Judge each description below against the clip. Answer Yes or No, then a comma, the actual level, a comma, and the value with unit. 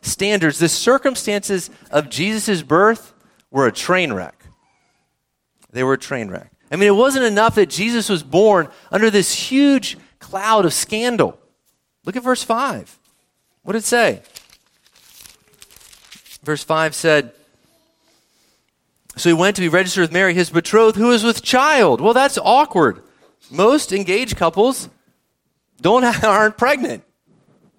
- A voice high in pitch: Yes, high, 205 Hz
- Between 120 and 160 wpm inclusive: Yes, average, 140 wpm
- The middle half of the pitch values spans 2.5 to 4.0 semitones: No, average, 5.3 semitones